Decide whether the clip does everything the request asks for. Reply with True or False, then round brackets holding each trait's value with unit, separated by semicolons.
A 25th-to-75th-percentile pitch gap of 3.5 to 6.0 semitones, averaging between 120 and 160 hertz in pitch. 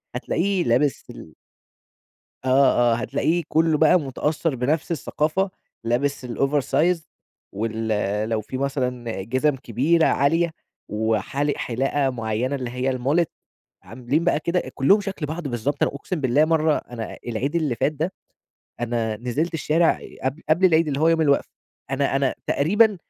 True (4.5 semitones; 140 Hz)